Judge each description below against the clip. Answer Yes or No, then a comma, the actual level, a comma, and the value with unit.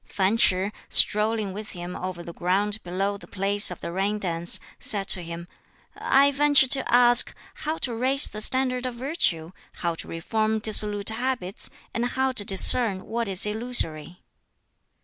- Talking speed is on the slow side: No, average, 165 wpm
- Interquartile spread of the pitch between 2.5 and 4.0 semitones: No, average, 4.8 semitones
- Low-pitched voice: No, high, 210 Hz